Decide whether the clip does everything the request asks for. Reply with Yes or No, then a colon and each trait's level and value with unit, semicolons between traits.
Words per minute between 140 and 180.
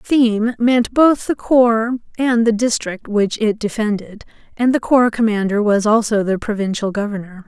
Yes: average, 160 wpm